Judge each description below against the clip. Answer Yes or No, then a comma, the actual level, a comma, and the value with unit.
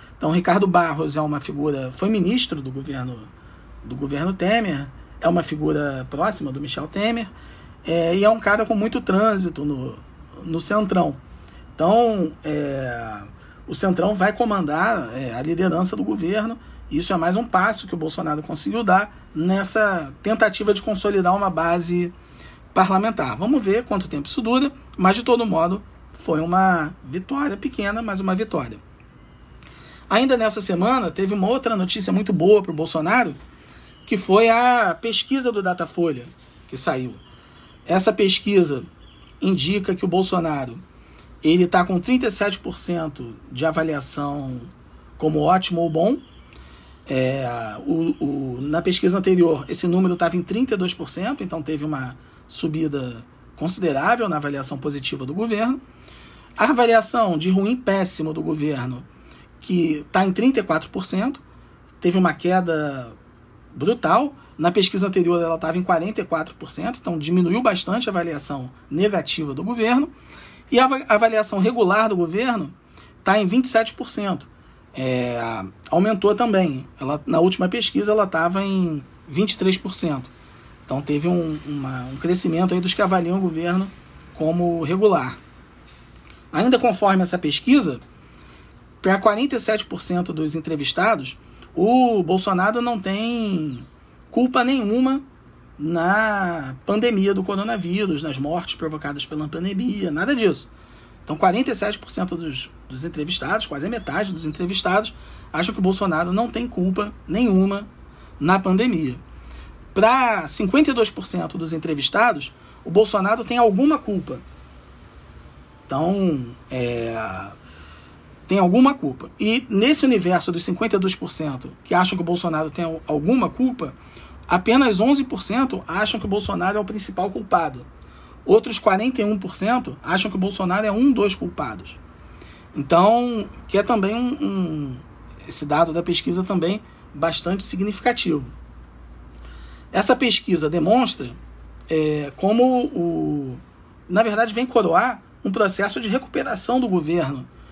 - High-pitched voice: No, medium, 180 Hz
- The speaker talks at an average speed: Yes, average, 130 wpm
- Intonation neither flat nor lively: No, wide, 6.2 semitones